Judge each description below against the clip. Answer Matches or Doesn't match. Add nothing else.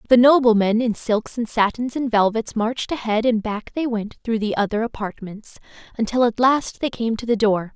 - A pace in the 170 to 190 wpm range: Doesn't match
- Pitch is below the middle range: Doesn't match